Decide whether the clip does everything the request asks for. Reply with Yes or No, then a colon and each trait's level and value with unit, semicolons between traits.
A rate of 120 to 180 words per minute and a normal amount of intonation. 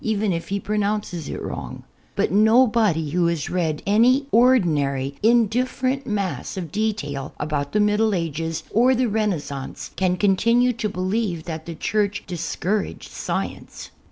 Yes: average, 165 wpm; average, 5.0 semitones